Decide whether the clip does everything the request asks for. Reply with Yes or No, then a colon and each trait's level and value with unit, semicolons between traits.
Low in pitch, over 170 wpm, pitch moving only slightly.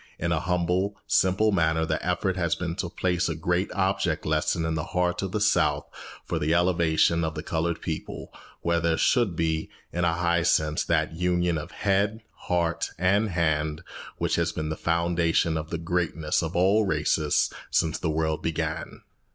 Yes: very low, 85 Hz; average, 180 wpm; narrow, 1.9 semitones